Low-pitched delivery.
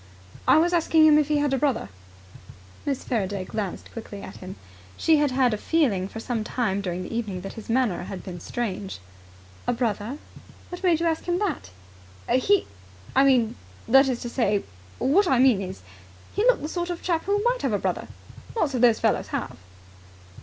No: very high, 255 Hz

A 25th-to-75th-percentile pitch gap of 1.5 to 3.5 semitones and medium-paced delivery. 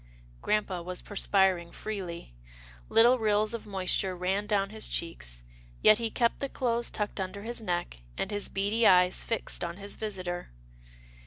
Yes: average, 3.1 semitones; average, 155 wpm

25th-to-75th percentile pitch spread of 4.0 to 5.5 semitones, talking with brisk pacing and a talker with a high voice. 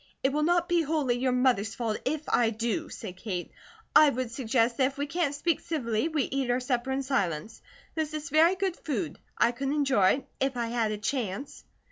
Yes: average, 4.5 semitones; fast, 210 wpm; very high, 265 Hz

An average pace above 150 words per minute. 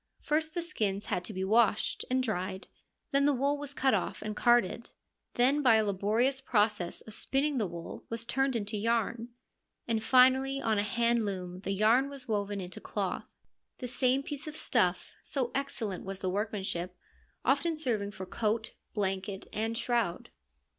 Yes: average, 170 wpm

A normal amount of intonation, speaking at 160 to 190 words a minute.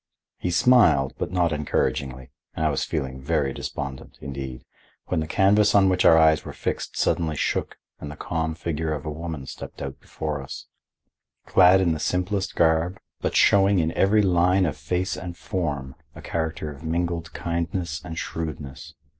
Yes: average, 3.4 semitones; average, 170 wpm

